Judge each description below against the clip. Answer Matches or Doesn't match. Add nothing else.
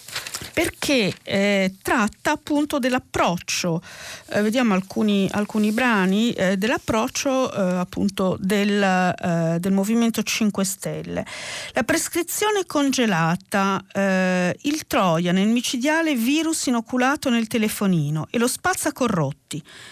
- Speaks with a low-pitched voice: Doesn't match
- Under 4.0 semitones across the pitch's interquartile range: Doesn't match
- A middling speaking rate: Doesn't match